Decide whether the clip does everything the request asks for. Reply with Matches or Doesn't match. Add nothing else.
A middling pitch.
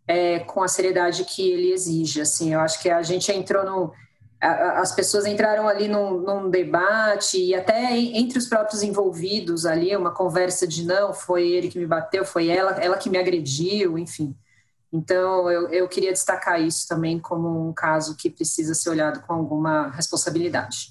Matches